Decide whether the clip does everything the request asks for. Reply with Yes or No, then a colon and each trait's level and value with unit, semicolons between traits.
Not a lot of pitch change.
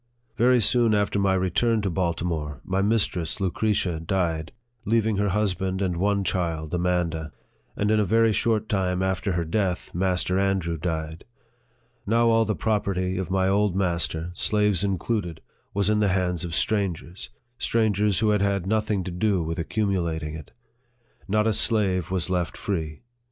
No: average, 3.4 semitones